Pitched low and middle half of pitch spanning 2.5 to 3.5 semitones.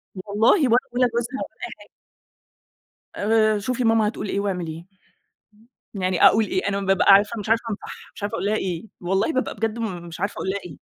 No: high, 205 Hz; average, 2.9 semitones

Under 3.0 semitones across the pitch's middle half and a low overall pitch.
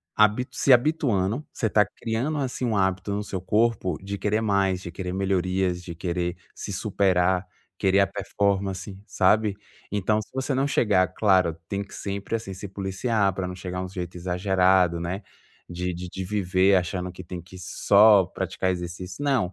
Yes: narrow, 2.6 semitones; very low, 95 Hz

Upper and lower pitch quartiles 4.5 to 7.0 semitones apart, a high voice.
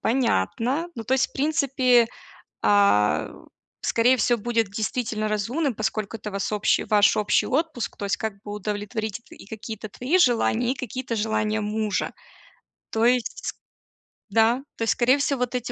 No: average, 2.9 semitones; high, 225 Hz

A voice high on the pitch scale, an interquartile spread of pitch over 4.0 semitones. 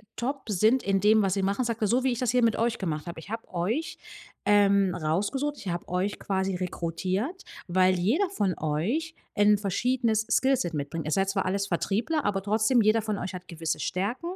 Yes: high, 205 Hz; average, 4.4 semitones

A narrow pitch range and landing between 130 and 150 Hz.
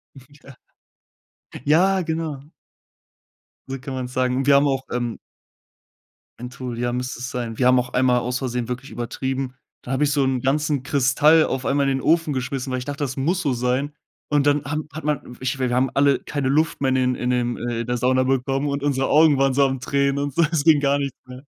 Yes: narrow, 2.2 semitones; low, 135 Hz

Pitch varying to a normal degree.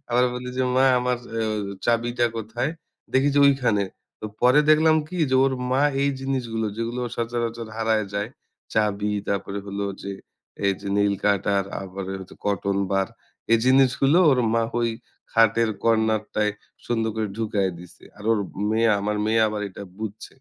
Yes: average, 3.2 semitones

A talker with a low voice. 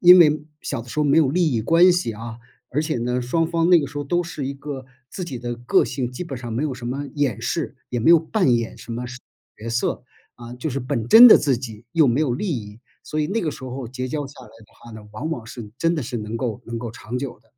Yes: low, 130 Hz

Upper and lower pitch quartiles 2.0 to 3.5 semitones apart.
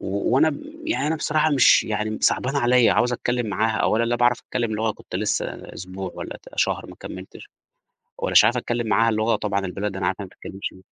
Yes: average, 3.0 semitones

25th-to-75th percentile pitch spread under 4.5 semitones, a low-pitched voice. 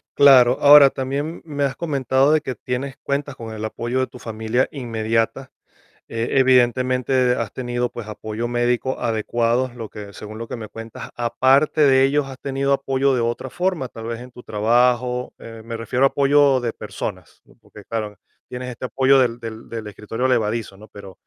Yes: average, 2.7 semitones; low, 125 Hz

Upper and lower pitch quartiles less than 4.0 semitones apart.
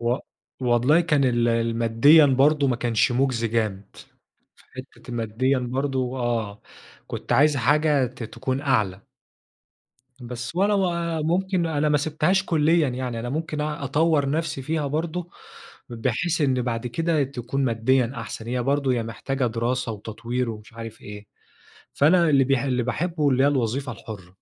No: average, 4.3 semitones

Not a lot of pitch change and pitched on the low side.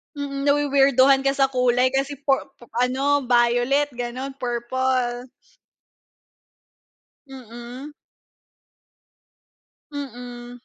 No: narrow, 2.2 semitones; very high, 260 Hz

